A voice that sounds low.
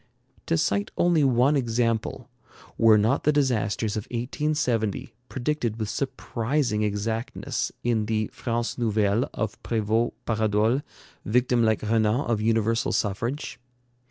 Yes: low, 115 Hz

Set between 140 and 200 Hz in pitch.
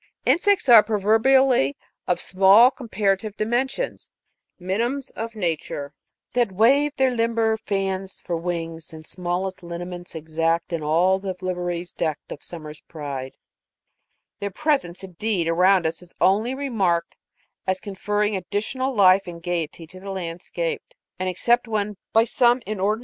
Yes: high, 190 Hz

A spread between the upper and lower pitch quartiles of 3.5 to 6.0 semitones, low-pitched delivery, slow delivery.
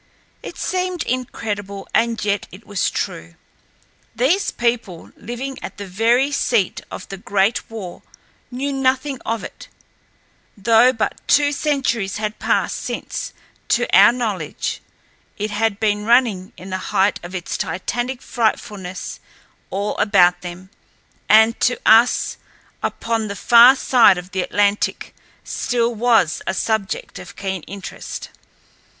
No: average, 3.9 semitones; high, 220 Hz; slow, 130 wpm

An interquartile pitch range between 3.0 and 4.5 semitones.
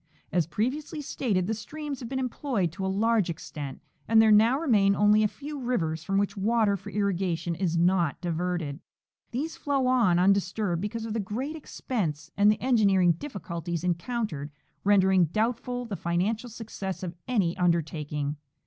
No: average, 5.2 semitones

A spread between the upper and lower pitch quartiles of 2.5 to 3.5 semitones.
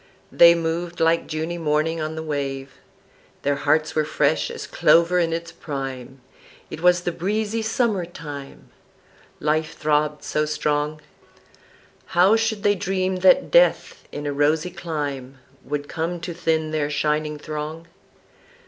Yes: average, 2.8 semitones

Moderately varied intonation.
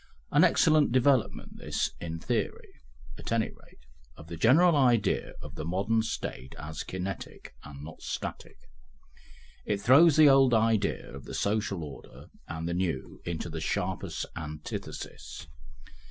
No: wide, 7.2 semitones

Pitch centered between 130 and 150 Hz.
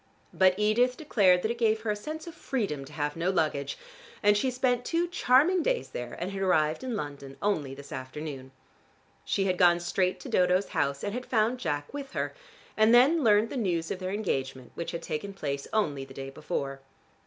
No: high, 190 Hz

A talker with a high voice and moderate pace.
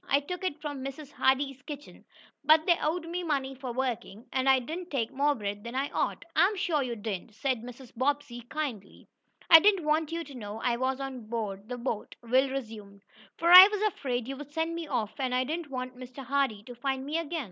No: very high, 270 Hz; fast, 215 wpm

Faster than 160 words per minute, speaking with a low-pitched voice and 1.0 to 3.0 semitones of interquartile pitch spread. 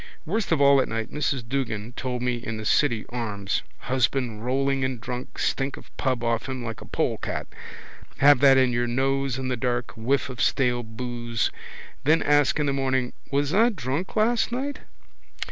Yes: average, 180 wpm; low, 130 Hz; narrow, 2.6 semitones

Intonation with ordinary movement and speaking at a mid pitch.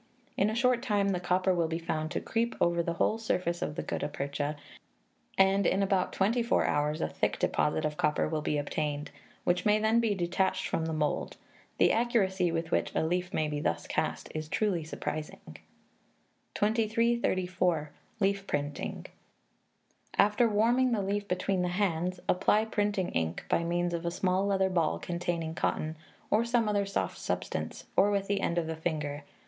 Yes: average, 4.2 semitones; medium, 180 Hz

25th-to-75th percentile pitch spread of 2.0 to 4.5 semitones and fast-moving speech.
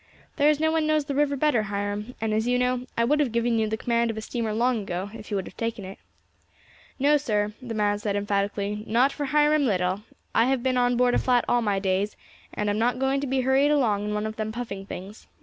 Yes: average, 4.1 semitones; fast, 255 wpm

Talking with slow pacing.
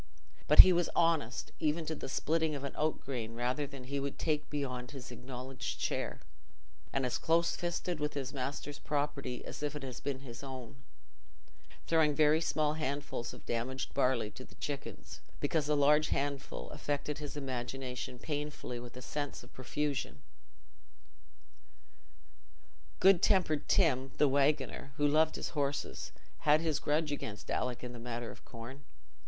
No: average, 160 wpm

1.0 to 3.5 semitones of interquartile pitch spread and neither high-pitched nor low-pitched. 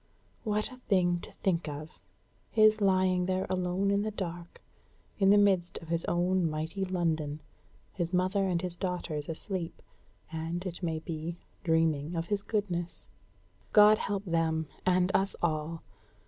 Yes: average, 2.8 semitones; medium, 180 Hz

